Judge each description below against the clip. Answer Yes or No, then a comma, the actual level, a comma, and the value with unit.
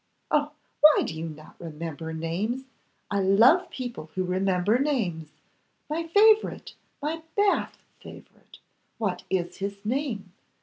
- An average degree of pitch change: No, wide, 9.0 semitones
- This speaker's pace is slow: Yes, slow, 125 wpm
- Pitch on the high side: Yes, high, 200 Hz